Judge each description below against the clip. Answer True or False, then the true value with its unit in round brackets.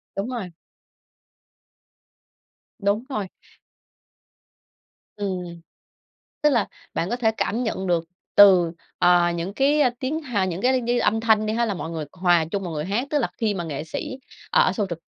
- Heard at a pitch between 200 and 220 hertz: True (205 Hz)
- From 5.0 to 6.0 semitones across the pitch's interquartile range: True (5.3 semitones)